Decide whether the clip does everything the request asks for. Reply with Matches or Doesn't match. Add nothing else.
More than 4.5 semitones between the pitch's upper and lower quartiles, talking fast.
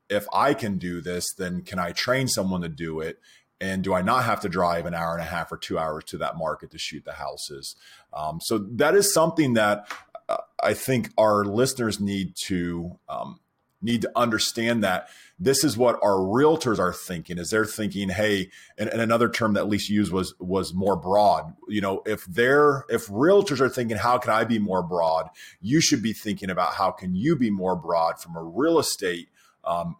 Matches